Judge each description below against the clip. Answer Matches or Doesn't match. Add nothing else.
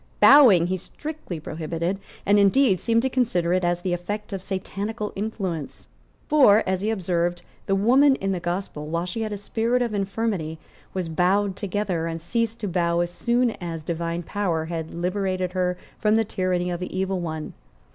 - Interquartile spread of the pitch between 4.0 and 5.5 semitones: Doesn't match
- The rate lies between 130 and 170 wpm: Doesn't match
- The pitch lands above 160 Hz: Matches